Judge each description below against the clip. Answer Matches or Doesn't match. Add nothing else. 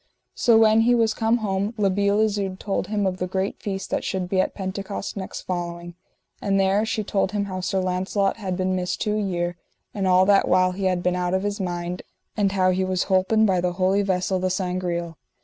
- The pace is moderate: Doesn't match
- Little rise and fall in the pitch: Matches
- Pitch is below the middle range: Doesn't match